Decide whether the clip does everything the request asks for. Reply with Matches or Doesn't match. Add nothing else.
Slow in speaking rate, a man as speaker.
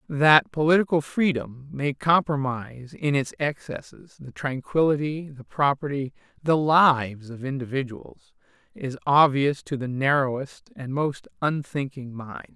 Matches